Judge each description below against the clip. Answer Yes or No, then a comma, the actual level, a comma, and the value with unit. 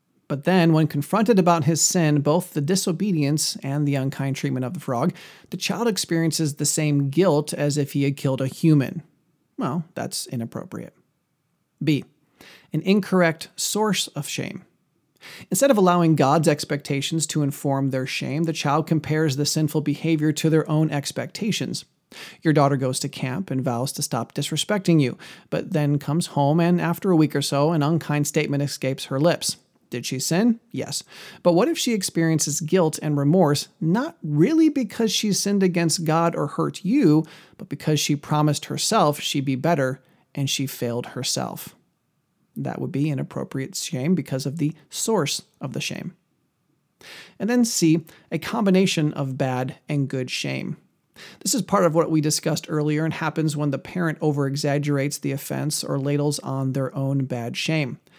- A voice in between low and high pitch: Yes, medium, 155 Hz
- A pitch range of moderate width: Yes, average, 3.3 semitones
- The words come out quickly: No, average, 170 wpm